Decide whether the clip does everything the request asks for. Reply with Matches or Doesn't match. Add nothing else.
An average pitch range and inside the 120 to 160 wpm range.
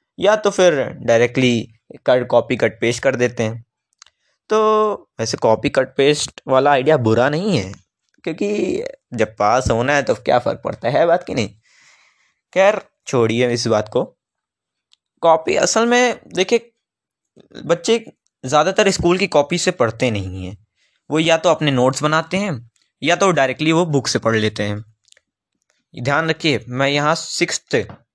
Doesn't match